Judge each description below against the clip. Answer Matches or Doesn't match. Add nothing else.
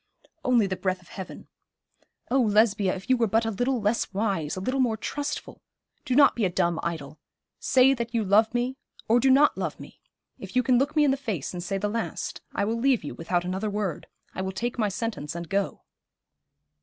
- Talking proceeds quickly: Matches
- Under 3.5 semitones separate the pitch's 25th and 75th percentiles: Doesn't match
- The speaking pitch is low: Doesn't match